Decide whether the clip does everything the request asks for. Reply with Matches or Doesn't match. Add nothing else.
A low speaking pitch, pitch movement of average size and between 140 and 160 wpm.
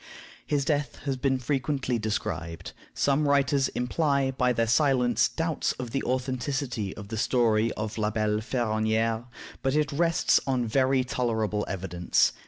Matches